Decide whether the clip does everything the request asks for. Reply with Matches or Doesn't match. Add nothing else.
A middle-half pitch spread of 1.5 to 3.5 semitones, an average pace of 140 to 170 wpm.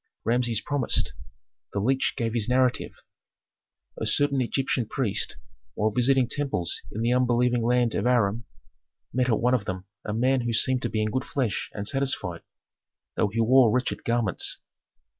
Matches